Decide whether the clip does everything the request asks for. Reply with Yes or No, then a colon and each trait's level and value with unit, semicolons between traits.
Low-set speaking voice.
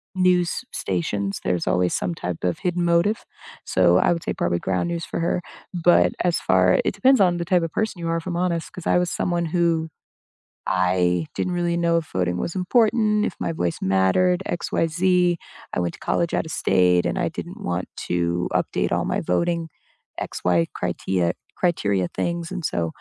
No: medium, 165 Hz